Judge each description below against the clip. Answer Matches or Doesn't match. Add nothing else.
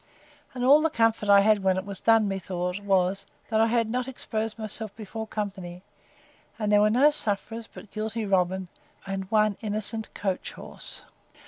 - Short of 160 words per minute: Doesn't match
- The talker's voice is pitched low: Doesn't match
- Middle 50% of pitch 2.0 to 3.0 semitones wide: Matches